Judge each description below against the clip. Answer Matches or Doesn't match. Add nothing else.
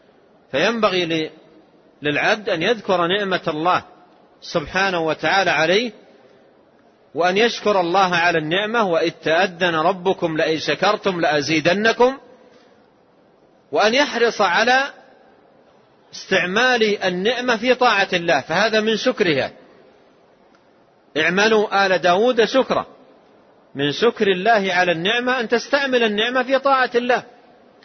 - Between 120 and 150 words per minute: Doesn't match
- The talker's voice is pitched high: Matches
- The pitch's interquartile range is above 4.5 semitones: Matches